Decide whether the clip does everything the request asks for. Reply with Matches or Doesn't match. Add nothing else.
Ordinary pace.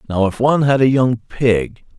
Doesn't match